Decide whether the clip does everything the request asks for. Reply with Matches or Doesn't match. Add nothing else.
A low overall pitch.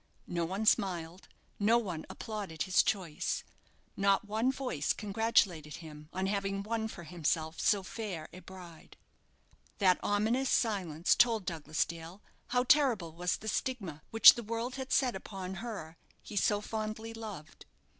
Doesn't match